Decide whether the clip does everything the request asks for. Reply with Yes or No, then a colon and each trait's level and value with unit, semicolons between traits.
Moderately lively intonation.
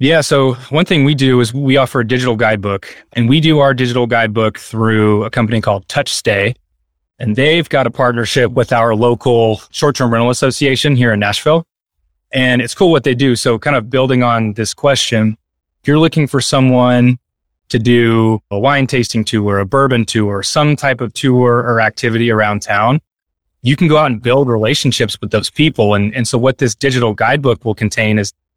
Yes: average, 3.6 semitones